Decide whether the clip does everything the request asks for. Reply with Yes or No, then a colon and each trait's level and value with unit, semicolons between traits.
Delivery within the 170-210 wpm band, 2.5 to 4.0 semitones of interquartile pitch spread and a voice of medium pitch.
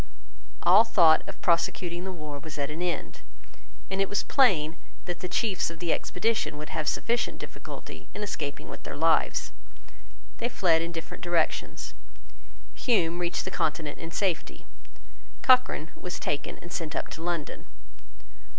No: average, 155 wpm; average, 3.1 semitones; medium, 170 Hz